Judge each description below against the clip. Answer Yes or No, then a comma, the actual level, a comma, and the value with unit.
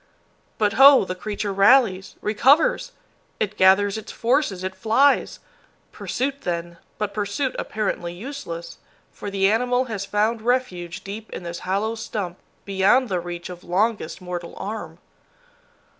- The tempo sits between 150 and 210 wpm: No, slow, 135 wpm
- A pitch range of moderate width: Yes, average, 4.0 semitones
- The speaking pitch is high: Yes, high, 205 Hz